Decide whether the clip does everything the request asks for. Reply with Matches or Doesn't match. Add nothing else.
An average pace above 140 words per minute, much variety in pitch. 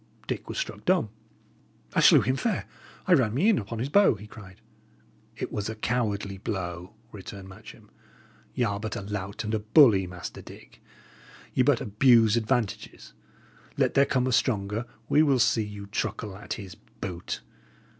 Doesn't match